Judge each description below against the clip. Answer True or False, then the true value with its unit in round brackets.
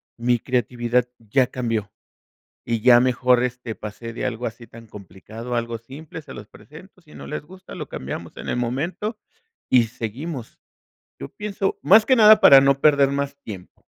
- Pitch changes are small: False (4.0 semitones)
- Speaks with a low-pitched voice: True (125 Hz)